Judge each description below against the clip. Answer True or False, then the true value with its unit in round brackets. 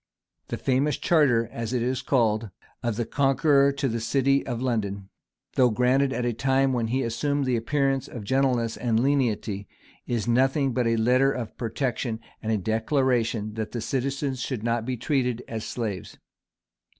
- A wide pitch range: False (2.9 semitones)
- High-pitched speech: False (125 Hz)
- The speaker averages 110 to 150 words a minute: False (175 wpm)